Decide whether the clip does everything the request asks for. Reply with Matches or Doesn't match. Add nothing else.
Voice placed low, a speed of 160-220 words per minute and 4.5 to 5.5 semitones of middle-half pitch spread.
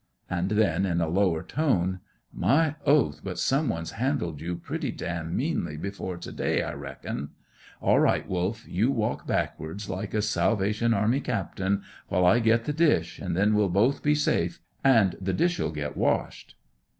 Matches